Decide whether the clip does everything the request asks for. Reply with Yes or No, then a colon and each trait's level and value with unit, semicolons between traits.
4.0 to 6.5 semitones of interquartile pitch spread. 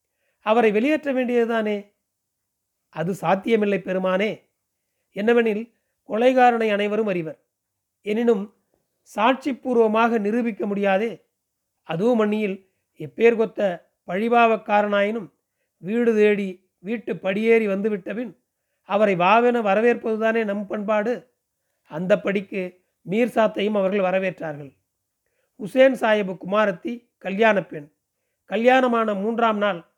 No: average, 3.3 semitones